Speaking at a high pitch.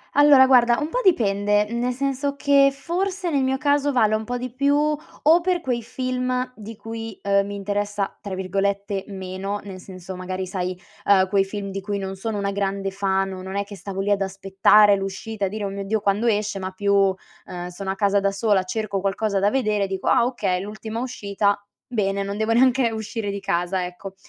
Yes: high, 205 Hz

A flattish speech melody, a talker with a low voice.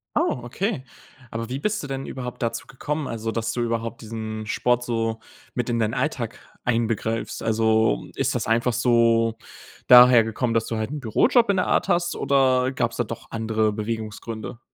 Yes: narrow, 2.2 semitones; low, 115 Hz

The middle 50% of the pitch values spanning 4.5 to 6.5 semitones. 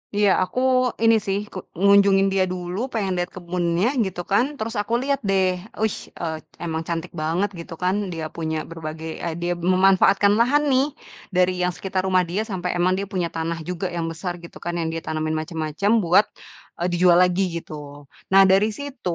No: average, 2.8 semitones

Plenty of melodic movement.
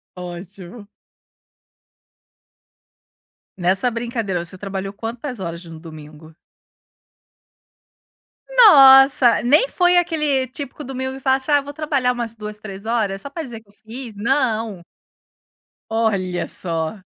Yes: wide, 5.8 semitones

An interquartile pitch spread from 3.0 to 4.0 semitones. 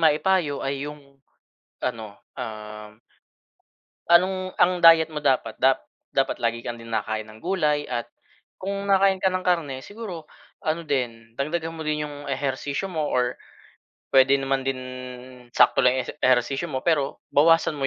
No: average, 4.8 semitones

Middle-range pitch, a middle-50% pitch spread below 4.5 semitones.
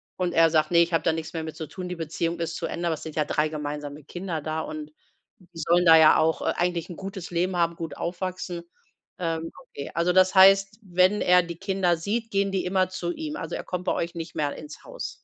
Yes: medium, 170 Hz; narrow, 2.4 semitones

